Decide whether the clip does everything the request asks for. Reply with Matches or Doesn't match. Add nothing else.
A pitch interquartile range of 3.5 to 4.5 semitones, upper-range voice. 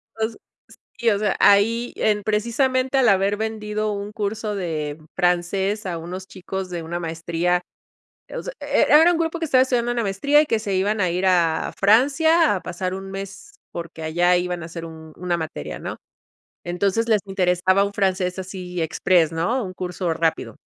Matches